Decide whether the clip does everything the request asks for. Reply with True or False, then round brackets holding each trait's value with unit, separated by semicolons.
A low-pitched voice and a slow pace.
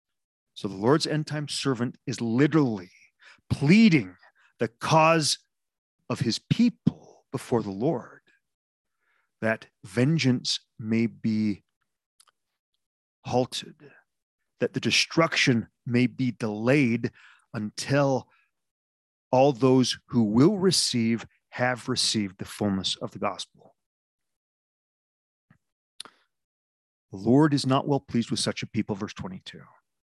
True (125 Hz; 105 wpm)